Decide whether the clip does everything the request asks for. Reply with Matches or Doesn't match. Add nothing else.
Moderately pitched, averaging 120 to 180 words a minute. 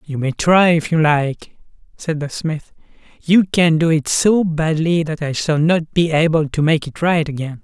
Doesn't match